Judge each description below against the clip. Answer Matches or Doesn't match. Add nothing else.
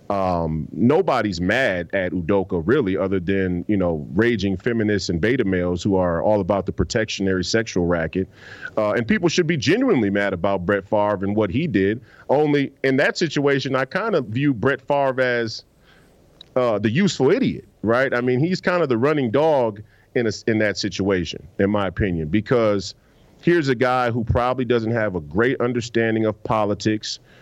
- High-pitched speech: Doesn't match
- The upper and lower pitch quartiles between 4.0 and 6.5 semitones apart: Matches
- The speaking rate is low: Doesn't match